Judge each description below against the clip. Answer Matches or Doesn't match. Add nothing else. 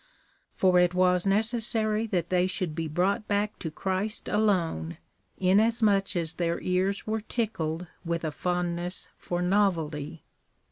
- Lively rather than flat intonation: Doesn't match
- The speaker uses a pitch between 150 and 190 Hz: Matches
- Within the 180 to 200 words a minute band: Doesn't match